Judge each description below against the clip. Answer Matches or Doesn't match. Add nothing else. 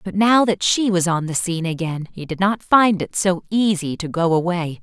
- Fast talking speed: Matches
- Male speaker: Doesn't match